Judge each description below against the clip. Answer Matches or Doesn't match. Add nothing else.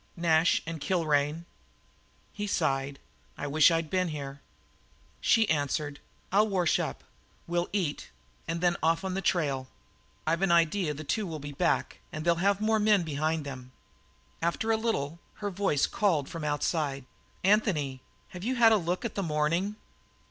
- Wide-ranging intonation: Doesn't match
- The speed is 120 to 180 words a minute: Matches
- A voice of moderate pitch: Matches